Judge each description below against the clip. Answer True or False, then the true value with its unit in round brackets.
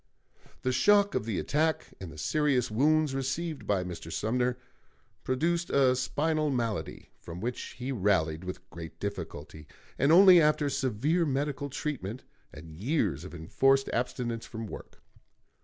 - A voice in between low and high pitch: False (125 Hz)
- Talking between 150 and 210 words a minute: False (140 wpm)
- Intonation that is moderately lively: False (7.5 semitones)